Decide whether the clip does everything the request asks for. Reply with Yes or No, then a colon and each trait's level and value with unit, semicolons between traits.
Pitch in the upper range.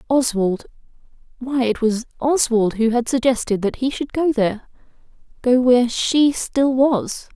Yes: high, 245 Hz